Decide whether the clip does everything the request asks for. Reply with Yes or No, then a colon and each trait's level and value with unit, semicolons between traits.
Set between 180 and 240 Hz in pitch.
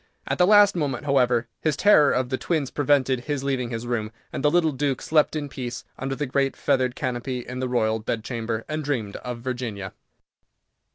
No: low, 130 Hz